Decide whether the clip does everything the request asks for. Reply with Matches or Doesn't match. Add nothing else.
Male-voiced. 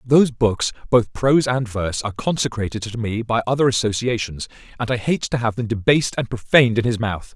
Matches